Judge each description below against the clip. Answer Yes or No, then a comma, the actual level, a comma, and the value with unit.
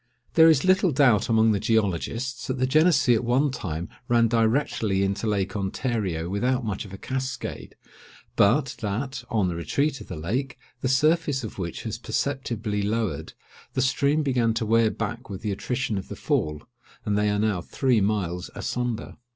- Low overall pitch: Yes, low, 115 Hz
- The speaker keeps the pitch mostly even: No, average, 4.5 semitones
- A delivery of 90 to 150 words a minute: No, average, 175 wpm